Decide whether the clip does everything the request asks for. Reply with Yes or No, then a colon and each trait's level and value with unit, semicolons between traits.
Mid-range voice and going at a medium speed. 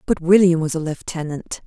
Yes: medium, 165 Hz; average, 180 wpm